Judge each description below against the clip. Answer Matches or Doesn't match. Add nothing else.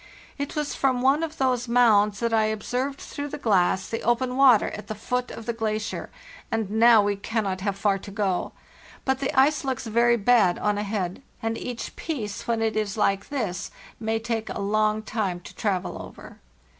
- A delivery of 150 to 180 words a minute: Doesn't match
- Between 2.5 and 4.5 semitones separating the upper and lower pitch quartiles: Matches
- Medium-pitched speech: Doesn't match